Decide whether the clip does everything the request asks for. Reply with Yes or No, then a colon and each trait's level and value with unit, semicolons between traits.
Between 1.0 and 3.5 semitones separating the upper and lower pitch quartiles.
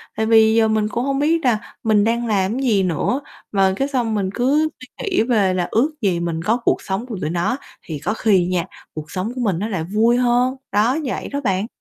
No: average, 4.4 semitones